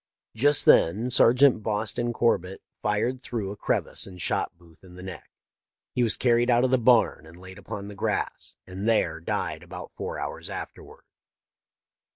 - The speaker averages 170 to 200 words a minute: Yes, average, 180 wpm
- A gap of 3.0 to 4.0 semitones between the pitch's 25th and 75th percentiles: No, average, 4.5 semitones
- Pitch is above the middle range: No, low, 105 Hz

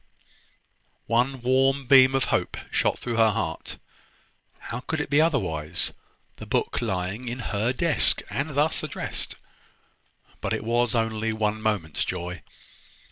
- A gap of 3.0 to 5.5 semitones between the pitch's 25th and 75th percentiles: Yes, average, 3.9 semitones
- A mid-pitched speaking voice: No, low, 115 Hz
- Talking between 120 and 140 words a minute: Yes, slow, 135 wpm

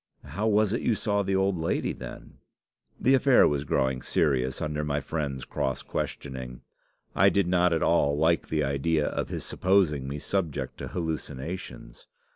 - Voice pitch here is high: No, very low, 80 Hz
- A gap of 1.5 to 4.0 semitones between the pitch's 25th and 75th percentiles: No, wide, 5.5 semitones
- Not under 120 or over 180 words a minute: Yes, average, 165 wpm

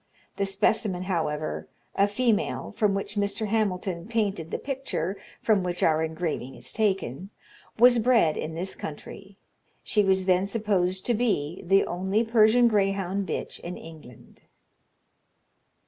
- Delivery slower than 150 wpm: Yes, slow, 135 wpm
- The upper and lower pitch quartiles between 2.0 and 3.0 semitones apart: No, average, 3.6 semitones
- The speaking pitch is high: Yes, high, 195 Hz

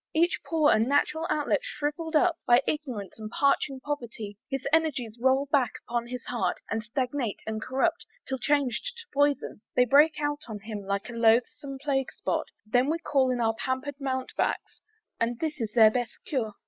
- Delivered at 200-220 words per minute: No, average, 180 wpm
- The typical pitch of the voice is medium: No, very high, 260 Hz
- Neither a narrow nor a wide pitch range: Yes, average, 4.1 semitones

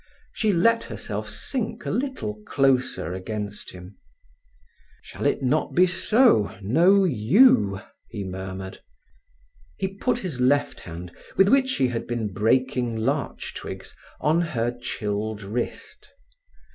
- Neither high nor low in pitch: No, low, 125 Hz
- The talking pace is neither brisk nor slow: No, slow, 120 wpm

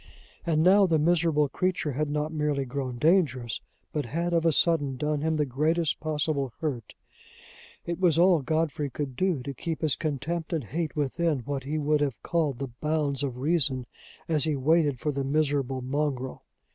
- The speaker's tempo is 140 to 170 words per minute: No, average, 180 wpm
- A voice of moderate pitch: Yes, medium, 150 Hz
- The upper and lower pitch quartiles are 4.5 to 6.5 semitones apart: No, average, 2.9 semitones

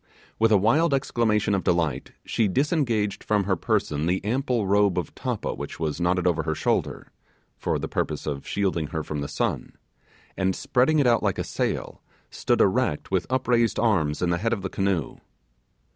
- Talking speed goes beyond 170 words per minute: Yes, average, 185 wpm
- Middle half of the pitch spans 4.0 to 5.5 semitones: Yes, average, 5.2 semitones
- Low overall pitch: Yes, low, 100 Hz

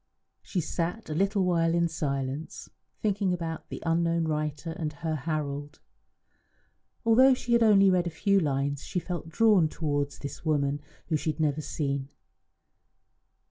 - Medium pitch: Yes, medium, 160 Hz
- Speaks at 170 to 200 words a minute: No, average, 150 wpm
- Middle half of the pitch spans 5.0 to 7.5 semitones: No, average, 3.7 semitones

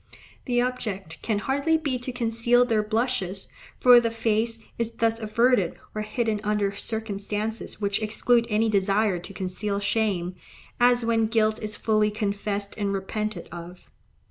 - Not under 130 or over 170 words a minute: Yes, average, 145 wpm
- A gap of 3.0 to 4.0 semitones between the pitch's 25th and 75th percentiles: No, narrow, 2.5 semitones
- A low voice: No, high, 215 Hz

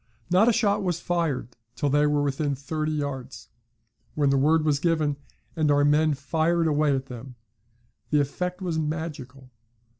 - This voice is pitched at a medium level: Yes, medium, 150 Hz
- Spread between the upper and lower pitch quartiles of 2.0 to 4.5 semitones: Yes, narrow, 2.6 semitones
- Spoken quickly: No, average, 160 wpm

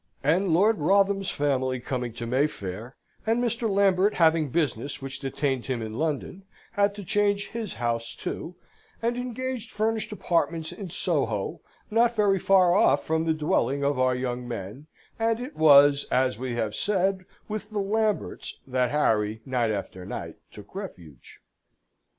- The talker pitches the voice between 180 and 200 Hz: No, medium, 155 Hz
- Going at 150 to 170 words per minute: Yes, average, 155 wpm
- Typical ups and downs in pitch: No, wide, 8.1 semitones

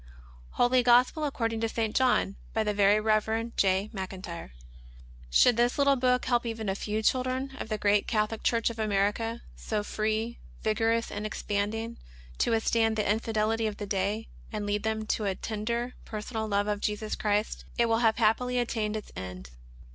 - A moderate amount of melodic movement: No, narrow, 1.9 semitones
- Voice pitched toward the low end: No, high, 220 Hz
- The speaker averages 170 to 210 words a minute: Yes, average, 175 wpm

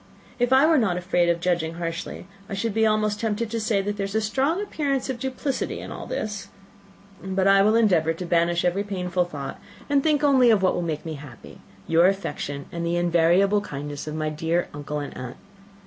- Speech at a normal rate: No, fast, 210 wpm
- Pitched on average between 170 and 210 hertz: Yes, high, 190 Hz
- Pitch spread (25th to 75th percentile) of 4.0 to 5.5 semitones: Yes, average, 4.8 semitones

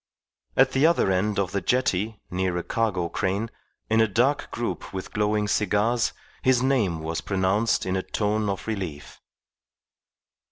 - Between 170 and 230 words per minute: No, average, 155 wpm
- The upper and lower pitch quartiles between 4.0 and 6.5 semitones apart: No, average, 3.4 semitones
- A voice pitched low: Yes, low, 105 Hz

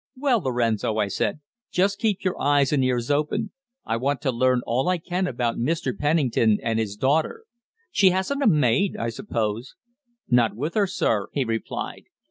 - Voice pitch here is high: No, low, 135 Hz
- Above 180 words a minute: No, average, 175 wpm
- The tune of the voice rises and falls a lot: Yes, wide, 7.6 semitones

